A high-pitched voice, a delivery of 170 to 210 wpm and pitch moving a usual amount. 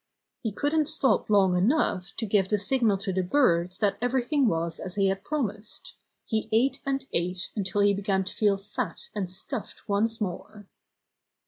Yes: high, 205 Hz; average, 175 wpm; average, 4.2 semitones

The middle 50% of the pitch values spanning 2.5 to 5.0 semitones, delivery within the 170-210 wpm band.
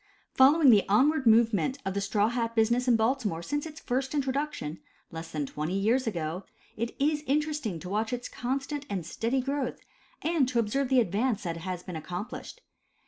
No: wide, 5.6 semitones; average, 180 wpm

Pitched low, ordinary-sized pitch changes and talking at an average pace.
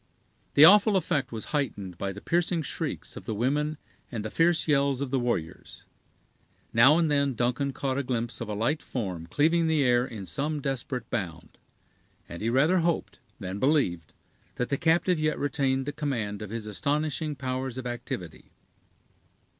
Yes: low, 130 Hz; average, 4.9 semitones; average, 170 wpm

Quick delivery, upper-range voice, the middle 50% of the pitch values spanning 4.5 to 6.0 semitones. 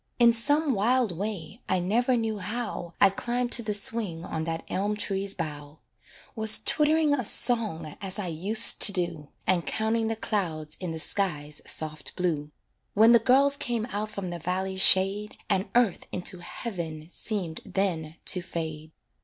No: average, 165 wpm; high, 195 Hz; average, 5.2 semitones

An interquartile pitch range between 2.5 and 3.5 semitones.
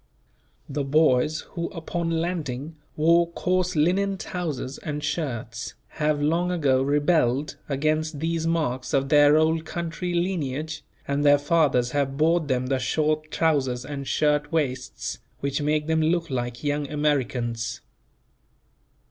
Yes: average, 3.0 semitones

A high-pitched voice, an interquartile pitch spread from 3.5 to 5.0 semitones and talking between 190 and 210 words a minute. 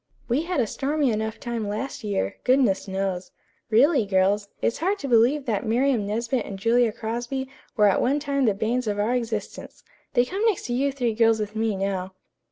Yes: high, 230 Hz; average, 4.2 semitones; average, 200 wpm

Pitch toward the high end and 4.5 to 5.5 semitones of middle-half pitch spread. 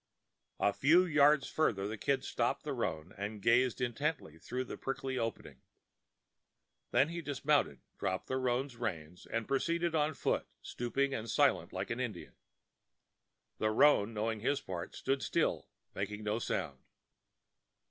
No: low, 120 Hz; average, 5.0 semitones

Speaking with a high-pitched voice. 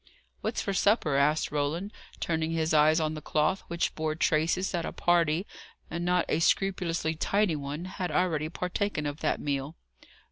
No: medium, 160 Hz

